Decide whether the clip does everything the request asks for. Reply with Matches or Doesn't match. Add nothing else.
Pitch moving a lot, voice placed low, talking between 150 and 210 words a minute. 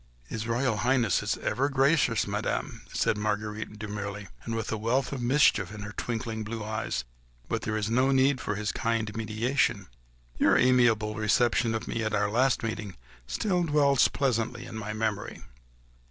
Doesn't match